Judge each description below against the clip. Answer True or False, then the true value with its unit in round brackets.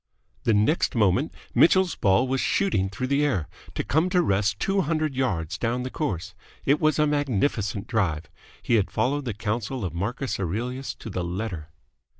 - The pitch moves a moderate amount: False (6.9 semitones)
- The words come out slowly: False (175 wpm)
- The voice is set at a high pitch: False (120 Hz)